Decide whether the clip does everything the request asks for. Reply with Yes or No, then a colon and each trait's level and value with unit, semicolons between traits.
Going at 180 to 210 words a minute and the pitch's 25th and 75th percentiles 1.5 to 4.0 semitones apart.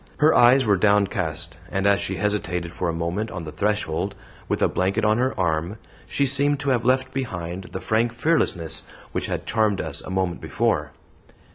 No: average, 190 wpm; wide, 5.4 semitones